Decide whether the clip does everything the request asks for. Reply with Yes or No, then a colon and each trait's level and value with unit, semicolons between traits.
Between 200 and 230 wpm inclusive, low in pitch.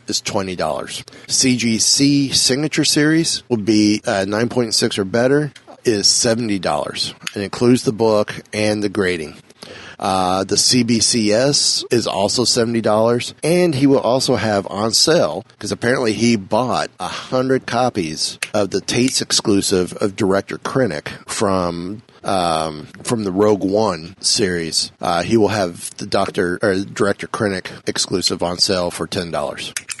No: slow, 135 wpm; low, 110 Hz